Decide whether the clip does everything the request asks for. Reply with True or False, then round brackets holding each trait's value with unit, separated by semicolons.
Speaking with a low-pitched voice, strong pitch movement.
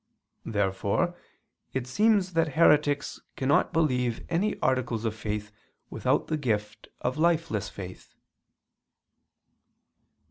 True (130 Hz; 7.5 semitones)